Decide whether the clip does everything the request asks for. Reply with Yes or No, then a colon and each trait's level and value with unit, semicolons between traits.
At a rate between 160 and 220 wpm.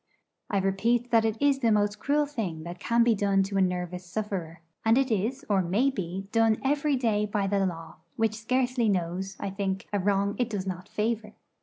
Yes: fast, 205 wpm